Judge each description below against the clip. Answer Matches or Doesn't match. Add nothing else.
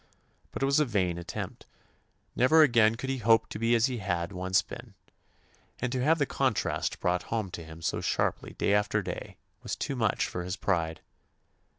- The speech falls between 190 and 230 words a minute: Matches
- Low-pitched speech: Matches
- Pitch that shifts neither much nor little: Doesn't match